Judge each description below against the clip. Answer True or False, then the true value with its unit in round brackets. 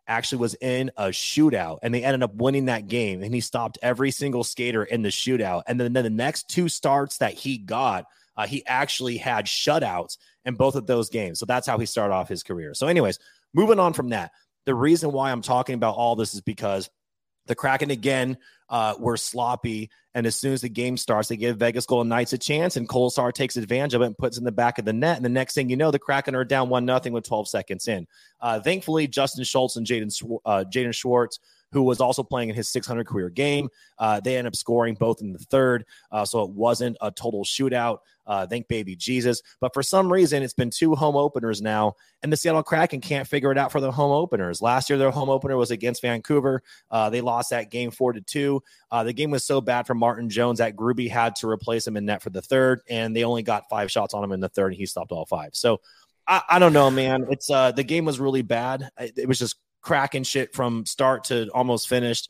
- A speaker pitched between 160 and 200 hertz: False (125 Hz)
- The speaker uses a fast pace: True (240 wpm)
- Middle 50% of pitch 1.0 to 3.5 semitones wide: True (2.7 semitones)